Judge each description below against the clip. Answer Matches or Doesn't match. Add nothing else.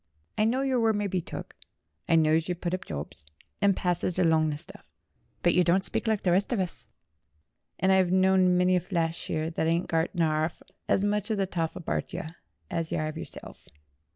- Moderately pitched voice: Matches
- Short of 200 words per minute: Doesn't match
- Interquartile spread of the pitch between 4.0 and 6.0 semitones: Doesn't match